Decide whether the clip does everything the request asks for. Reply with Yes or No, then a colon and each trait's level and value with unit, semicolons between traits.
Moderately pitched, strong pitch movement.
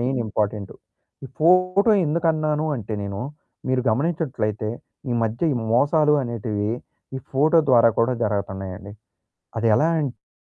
No: low, 125 Hz; wide, 6.4 semitones